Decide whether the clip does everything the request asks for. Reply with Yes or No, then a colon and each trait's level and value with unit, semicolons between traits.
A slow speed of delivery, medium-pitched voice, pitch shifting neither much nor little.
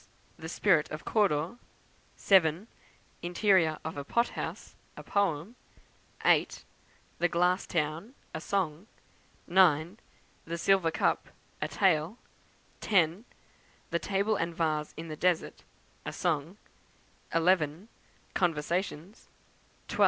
Yes: slow, 110 wpm; medium, 170 Hz; average, 3.6 semitones